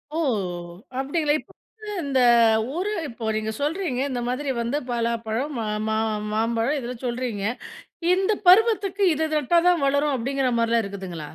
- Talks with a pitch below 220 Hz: No, very high, 265 Hz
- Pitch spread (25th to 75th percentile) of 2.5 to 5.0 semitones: No, wide, 5.4 semitones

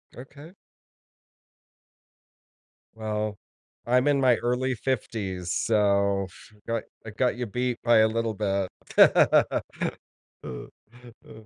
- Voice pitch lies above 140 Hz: No, low, 115 Hz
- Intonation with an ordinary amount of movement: Yes, average, 3.0 semitones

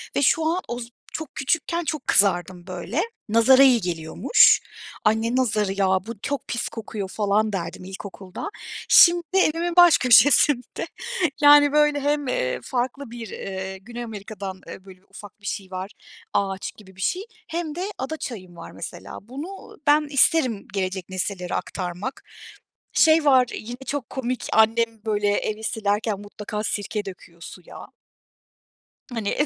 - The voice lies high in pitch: Yes, high, 220 Hz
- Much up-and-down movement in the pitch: Yes, wide, 6.2 semitones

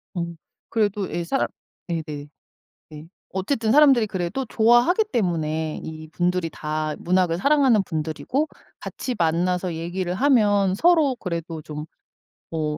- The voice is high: No, medium, 180 Hz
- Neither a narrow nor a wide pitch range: No, wide, 6.2 semitones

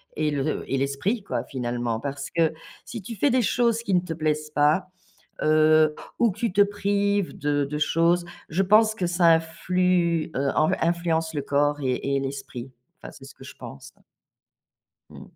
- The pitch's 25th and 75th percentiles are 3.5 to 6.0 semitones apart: Yes, average, 4.9 semitones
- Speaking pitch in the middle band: Yes, medium, 160 Hz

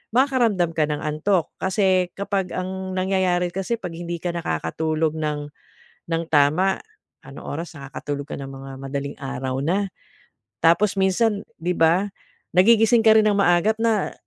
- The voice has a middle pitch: Yes, medium, 175 Hz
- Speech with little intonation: No, average, 4.5 semitones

